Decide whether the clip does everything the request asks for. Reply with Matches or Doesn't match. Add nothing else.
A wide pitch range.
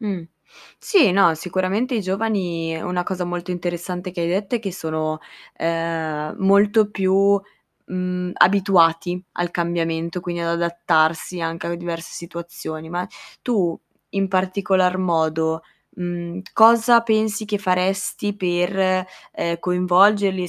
Doesn't match